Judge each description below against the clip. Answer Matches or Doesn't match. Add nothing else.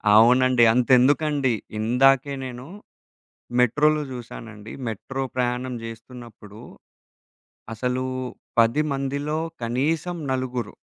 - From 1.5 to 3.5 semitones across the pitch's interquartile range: Matches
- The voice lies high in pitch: Doesn't match